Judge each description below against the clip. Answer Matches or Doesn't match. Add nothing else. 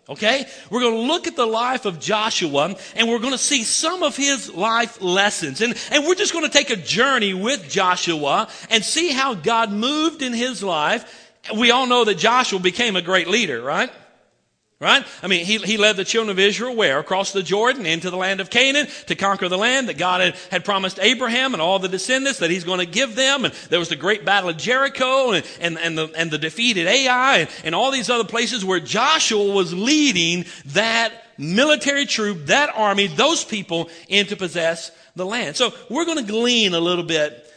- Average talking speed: Doesn't match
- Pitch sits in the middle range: Doesn't match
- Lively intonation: Matches